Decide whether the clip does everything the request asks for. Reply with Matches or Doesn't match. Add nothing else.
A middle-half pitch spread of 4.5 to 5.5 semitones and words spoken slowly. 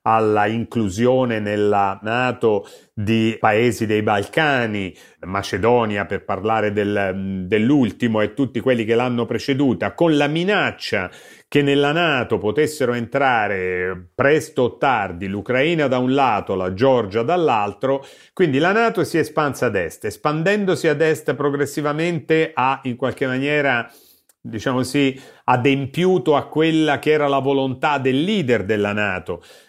Doesn't match